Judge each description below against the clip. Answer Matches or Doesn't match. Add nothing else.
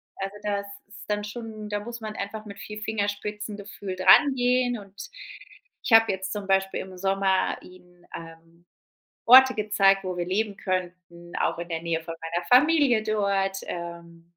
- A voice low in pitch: Doesn't match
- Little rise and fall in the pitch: Doesn't match